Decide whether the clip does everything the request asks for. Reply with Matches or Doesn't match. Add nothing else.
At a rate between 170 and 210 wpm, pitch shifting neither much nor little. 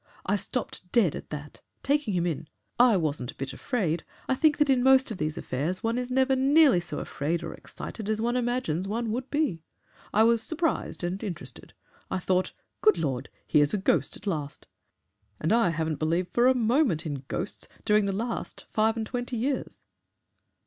Doesn't match